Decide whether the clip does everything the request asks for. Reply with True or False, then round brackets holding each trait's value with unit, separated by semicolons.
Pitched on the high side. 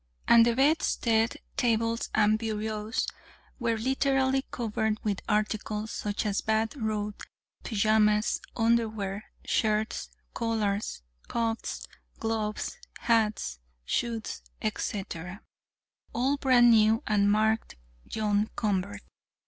True (220 Hz)